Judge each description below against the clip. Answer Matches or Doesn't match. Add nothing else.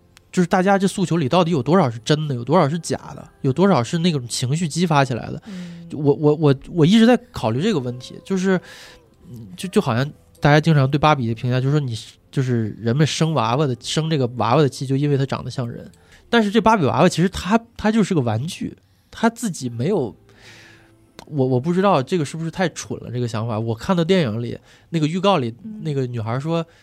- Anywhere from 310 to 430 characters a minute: Matches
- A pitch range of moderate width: Doesn't match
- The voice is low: Doesn't match